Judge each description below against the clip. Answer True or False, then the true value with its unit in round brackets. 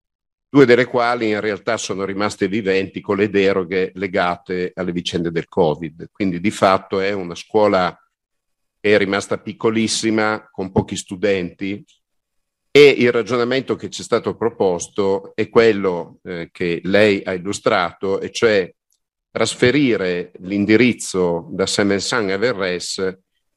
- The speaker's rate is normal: True (130 wpm)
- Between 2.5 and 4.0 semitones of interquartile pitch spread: True (2.9 semitones)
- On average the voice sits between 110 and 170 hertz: False (100 Hz)